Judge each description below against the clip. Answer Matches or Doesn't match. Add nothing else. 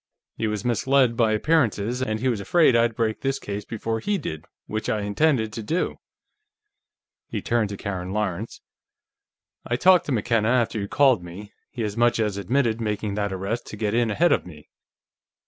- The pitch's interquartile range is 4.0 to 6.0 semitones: Doesn't match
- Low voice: Matches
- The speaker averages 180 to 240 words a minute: Matches